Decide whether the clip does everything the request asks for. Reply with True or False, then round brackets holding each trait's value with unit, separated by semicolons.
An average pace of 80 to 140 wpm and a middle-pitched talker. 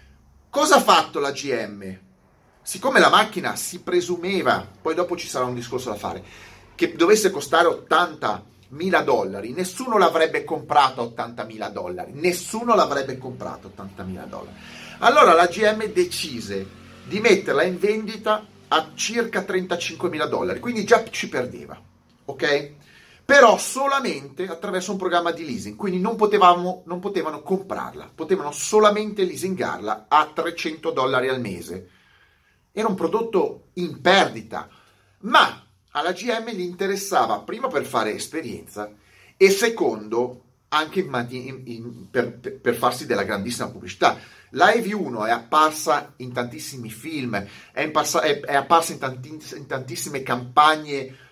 True (135 wpm; 165 Hz)